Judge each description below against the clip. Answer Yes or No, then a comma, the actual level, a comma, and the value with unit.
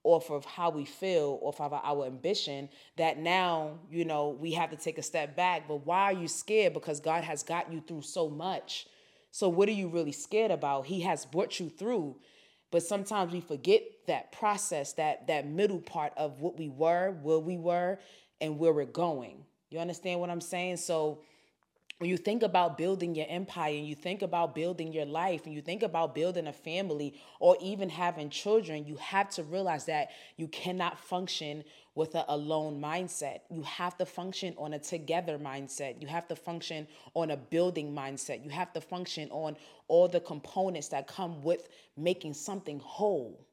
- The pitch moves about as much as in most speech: Yes, average, 3.0 semitones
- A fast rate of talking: No, average, 190 wpm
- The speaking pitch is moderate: Yes, medium, 165 Hz